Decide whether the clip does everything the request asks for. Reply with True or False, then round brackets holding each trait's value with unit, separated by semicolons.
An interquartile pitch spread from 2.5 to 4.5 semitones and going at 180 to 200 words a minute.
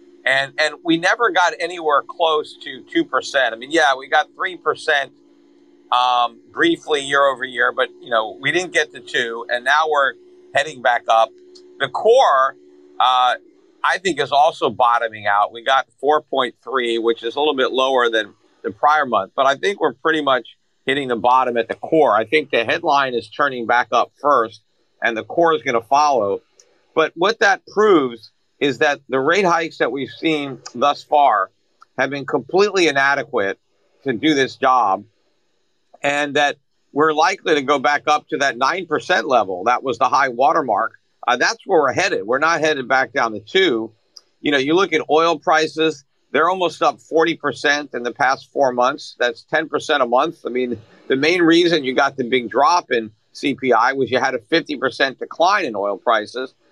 False (5.0 semitones; 190 wpm)